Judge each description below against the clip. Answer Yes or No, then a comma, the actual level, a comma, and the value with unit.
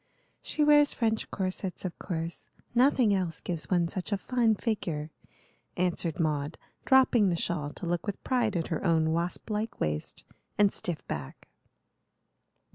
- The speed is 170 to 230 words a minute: No, average, 150 wpm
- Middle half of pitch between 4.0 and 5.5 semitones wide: Yes, average, 5.0 semitones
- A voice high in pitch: No, medium, 180 Hz